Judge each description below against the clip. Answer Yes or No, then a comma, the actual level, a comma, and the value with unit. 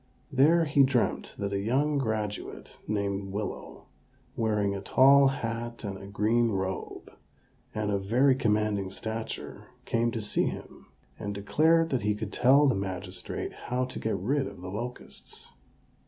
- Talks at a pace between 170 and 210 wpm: No, average, 155 wpm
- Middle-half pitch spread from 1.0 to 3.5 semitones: No, average, 4.5 semitones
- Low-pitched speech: Yes, low, 110 Hz